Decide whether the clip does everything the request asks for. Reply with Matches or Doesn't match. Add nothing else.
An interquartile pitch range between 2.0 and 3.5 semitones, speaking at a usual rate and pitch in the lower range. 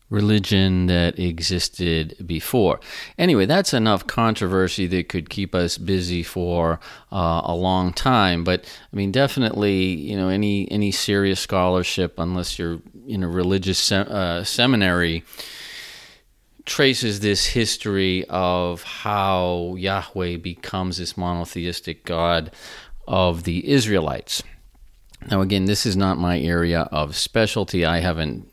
Doesn't match